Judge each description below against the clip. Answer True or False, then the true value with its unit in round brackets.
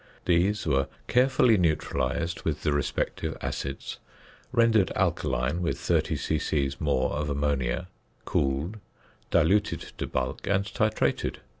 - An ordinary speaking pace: False (115 wpm)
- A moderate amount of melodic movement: False (6.4 semitones)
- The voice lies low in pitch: True (80 Hz)